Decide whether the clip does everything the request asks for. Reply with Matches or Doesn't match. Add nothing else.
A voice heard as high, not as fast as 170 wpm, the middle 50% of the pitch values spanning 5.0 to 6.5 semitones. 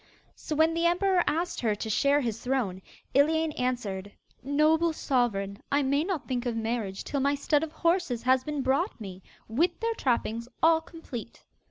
Doesn't match